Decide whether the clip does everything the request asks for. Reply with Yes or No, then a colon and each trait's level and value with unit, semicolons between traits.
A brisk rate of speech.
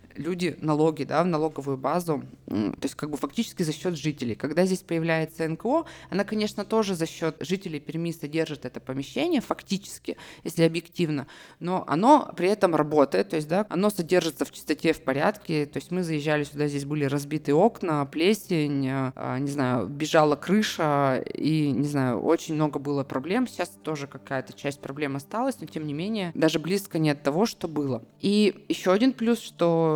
Yes: fast, 175 wpm